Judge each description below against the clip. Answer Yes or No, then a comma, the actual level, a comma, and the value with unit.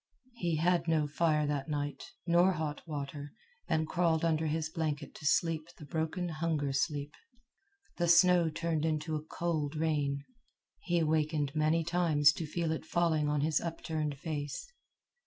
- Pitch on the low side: No, medium, 155 Hz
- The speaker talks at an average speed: Yes, average, 155 wpm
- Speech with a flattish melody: Yes, narrow, 2.0 semitones